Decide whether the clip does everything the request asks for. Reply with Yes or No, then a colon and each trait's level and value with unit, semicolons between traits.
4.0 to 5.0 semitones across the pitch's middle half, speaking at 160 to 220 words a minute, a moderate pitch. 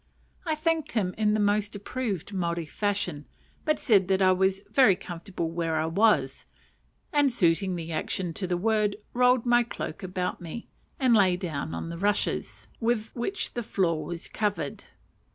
No: average, 4.5 semitones; average, 165 wpm; high, 200 Hz